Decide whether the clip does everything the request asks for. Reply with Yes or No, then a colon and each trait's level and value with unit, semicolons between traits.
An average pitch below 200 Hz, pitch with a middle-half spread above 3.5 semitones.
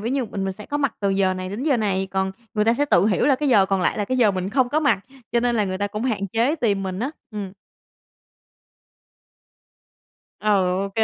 No: high, 210 Hz; average, 4.3 semitones